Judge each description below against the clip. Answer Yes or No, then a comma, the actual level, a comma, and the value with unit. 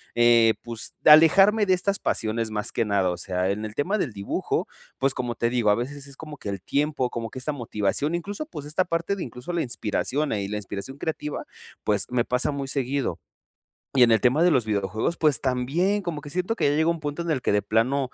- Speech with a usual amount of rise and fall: No, wide, 5.7 semitones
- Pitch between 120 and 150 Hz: Yes, low, 135 Hz